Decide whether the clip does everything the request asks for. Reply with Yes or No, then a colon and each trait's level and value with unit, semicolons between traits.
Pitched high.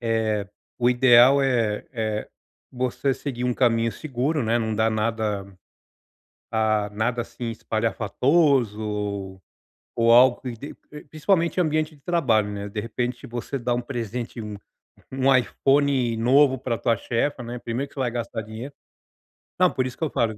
No: low, 120 Hz